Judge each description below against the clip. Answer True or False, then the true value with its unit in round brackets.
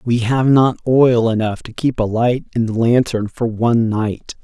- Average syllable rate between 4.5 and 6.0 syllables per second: False (4.3 syllables/s)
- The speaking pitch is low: True (115 Hz)